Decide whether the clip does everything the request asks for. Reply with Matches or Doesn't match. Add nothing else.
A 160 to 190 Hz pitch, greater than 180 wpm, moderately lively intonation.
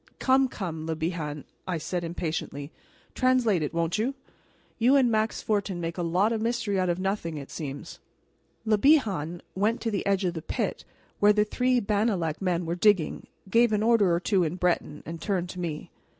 Matches